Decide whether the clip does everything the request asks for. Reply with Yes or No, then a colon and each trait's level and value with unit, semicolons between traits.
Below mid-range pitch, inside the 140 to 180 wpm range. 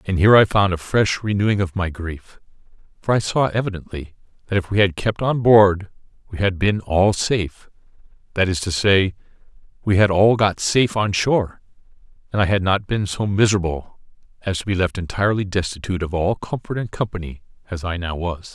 No: very low, 95 Hz; average, 190 wpm